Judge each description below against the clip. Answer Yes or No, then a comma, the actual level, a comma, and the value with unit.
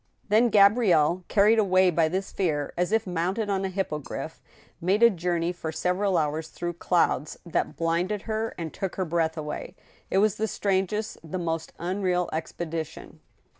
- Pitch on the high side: No, medium, 180 Hz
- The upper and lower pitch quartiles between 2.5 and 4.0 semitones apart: Yes, average, 3.3 semitones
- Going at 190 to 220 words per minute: No, average, 165 wpm